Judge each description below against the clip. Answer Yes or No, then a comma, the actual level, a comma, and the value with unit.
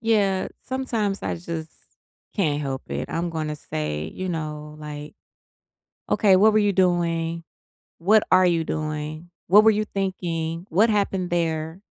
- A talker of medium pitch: Yes, medium, 170 Hz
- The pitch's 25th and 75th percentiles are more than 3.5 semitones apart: Yes, average, 4.0 semitones